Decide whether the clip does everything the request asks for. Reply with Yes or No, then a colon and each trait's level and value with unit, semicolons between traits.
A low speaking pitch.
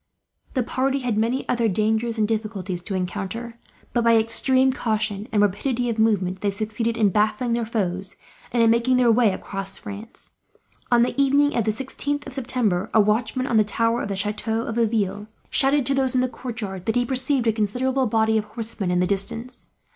No: high, 225 Hz